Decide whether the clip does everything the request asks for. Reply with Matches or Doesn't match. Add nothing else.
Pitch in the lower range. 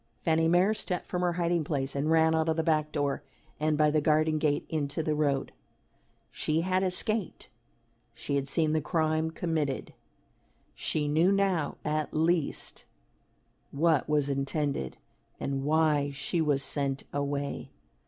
Doesn't match